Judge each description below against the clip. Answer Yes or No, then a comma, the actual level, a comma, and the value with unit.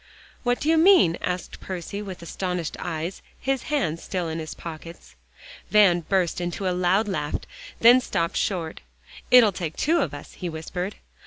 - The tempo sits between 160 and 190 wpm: Yes, average, 165 wpm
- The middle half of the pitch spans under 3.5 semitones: No, average, 4.0 semitones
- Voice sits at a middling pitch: Yes, medium, 180 Hz